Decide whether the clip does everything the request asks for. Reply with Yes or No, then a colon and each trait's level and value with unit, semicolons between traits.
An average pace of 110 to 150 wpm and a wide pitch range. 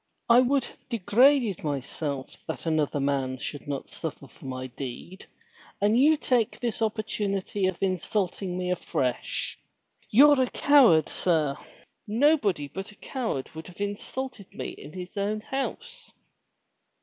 Yes: slow, 135 wpm; wide, 7.9 semitones